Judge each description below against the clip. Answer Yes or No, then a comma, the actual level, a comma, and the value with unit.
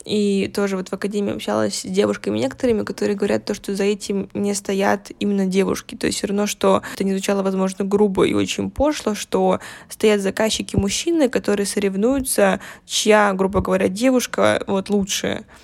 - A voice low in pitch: No, high, 200 Hz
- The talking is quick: Yes, fast, 170 wpm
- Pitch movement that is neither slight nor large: No, narrow, 1.5 semitones